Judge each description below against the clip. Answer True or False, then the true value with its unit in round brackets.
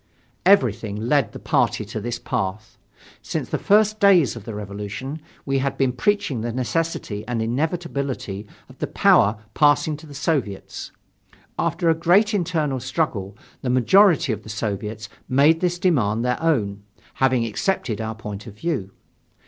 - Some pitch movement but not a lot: False (7.0 semitones)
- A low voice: True (130 Hz)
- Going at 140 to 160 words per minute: True (155 wpm)